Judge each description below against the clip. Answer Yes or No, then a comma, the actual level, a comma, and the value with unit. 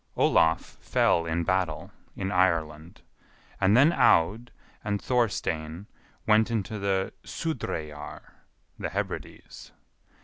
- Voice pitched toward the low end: Yes, very low, 95 Hz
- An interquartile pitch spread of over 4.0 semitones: Yes, average, 4.8 semitones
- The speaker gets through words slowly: Yes, slow, 100 wpm